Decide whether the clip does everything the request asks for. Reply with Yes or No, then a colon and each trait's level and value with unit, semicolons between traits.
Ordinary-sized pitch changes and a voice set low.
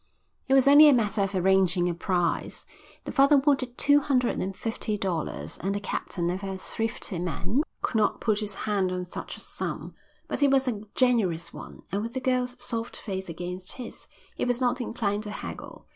No: average, 5.0 semitones; high, 210 Hz